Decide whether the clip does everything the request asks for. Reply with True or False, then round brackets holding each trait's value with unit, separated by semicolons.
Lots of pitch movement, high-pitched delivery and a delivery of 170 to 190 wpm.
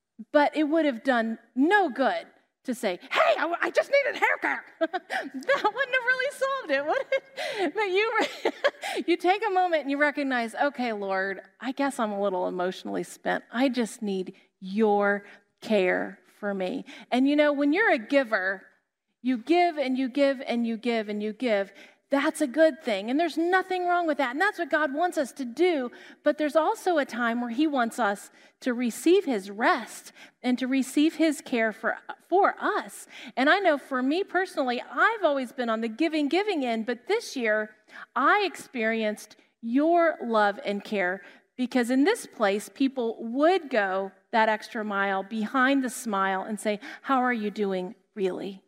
True (6.7 semitones; 265 Hz; 185 wpm)